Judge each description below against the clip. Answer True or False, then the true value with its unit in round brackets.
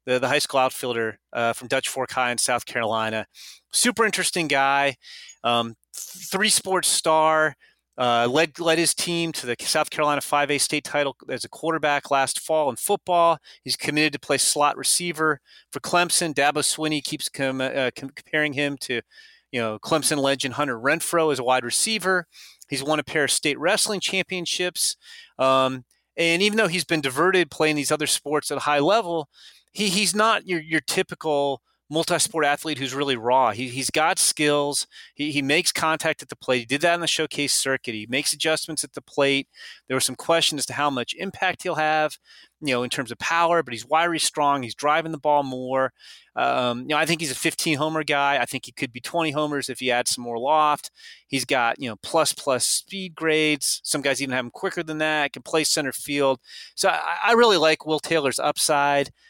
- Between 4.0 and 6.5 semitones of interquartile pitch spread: False (3.6 semitones)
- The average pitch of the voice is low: False (150 Hz)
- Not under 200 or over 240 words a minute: True (205 wpm)